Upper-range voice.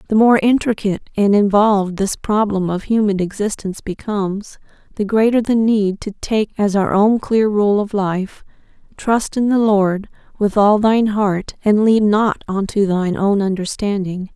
Yes: high, 205 Hz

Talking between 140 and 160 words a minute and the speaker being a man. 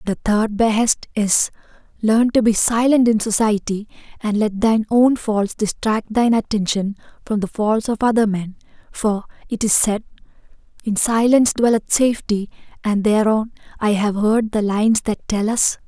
No: average, 155 wpm; female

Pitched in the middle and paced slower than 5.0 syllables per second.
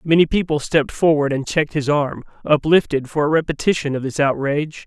No: medium, 150 Hz; 5.9 syllables/s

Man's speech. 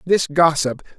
Yes: male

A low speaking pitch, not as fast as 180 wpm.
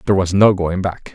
No: very low, 95 Hz; fast, 260 wpm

